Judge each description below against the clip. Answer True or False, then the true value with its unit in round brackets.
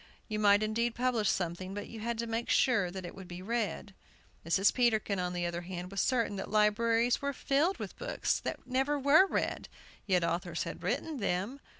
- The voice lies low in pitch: False (215 Hz)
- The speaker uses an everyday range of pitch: True (4.6 semitones)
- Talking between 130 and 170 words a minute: False (200 wpm)